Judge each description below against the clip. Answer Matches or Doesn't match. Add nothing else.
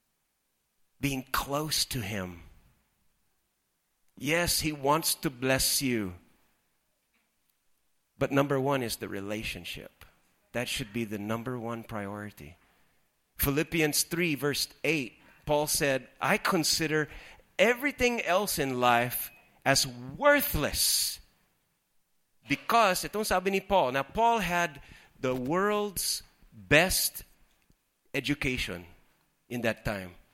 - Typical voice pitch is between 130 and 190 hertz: Matches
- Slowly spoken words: Matches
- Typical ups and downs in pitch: Doesn't match